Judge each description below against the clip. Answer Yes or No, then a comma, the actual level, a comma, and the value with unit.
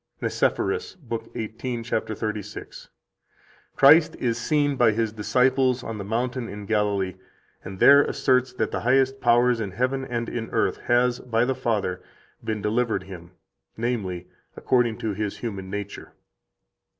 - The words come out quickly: No, average, 150 wpm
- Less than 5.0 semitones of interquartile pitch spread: Yes, average, 3.3 semitones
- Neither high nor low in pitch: No, low, 115 Hz